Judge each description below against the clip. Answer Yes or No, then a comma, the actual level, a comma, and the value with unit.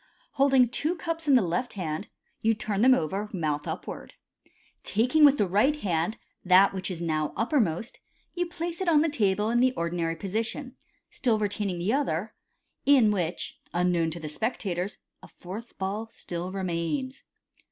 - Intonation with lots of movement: Yes, wide, 6.6 semitones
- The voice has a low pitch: No, high, 210 Hz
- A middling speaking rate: Yes, average, 165 wpm